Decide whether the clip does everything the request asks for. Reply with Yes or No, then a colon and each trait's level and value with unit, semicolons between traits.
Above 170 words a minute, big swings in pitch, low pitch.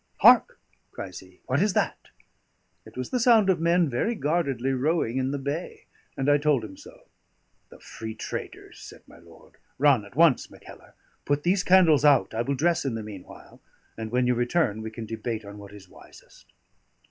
Yes: average, 190 wpm; wide, 6.4 semitones; low, 130 Hz